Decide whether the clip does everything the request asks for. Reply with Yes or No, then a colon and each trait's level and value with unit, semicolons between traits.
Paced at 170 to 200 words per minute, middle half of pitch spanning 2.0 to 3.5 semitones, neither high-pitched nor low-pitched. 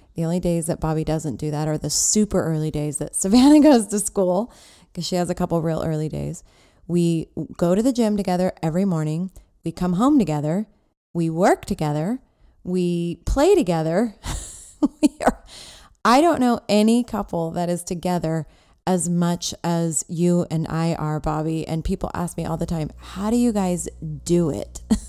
No: average, 180 wpm; average, 4.0 semitones; medium, 175 Hz